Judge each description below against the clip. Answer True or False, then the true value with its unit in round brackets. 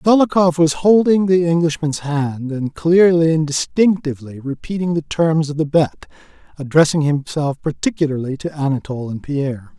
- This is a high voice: False (155 Hz)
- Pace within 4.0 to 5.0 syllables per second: True (4.8 syllables/s)